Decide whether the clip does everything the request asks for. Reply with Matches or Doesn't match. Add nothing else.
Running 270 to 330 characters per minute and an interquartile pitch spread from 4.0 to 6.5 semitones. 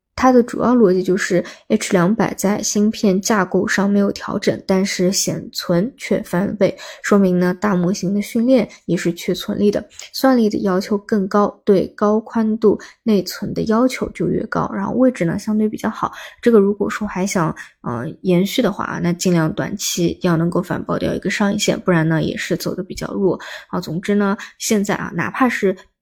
Doesn't match